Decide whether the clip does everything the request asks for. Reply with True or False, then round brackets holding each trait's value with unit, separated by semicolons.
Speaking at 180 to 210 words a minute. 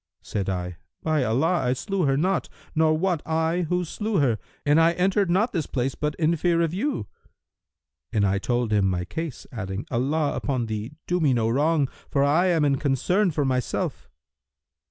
True (185 wpm)